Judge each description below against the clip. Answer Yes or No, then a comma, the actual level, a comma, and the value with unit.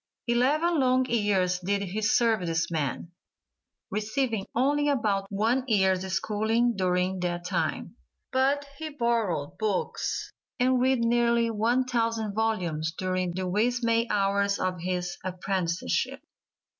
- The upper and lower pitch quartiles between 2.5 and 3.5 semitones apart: No, average, 4.5 semitones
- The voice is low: No, high, 210 Hz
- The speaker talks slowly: Yes, slow, 125 wpm